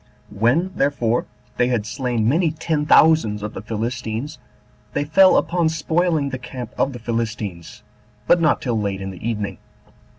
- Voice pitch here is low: Yes, low, 125 Hz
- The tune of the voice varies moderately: No, wide, 6.1 semitones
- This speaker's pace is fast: No, average, 165 wpm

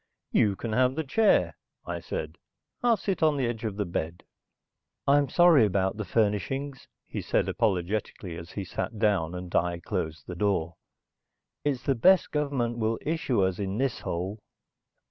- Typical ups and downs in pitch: No, wide, 6.5 semitones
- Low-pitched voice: Yes, low, 110 Hz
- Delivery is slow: No, average, 165 wpm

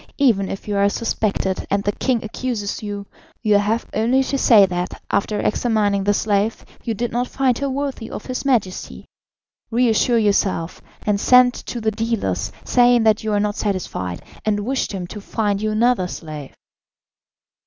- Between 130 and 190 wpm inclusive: Yes, average, 170 wpm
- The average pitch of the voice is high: Yes, high, 215 Hz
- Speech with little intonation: No, average, 3.2 semitones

